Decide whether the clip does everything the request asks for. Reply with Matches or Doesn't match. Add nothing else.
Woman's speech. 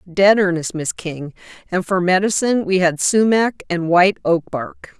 Matches